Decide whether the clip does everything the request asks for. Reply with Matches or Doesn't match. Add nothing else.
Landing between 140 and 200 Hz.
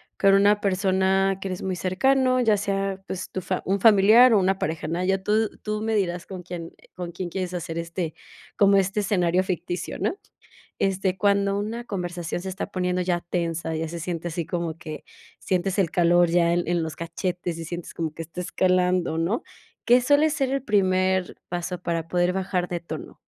Matches